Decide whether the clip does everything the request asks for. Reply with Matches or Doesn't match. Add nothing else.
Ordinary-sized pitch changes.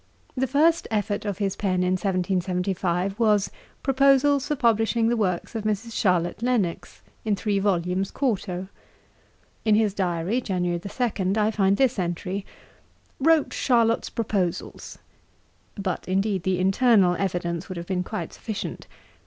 Matches